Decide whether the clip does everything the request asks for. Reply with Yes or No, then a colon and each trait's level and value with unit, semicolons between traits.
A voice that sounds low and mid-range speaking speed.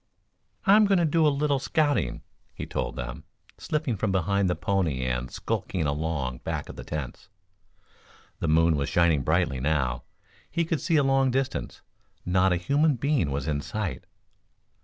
Yes: very low, 90 Hz; average, 165 wpm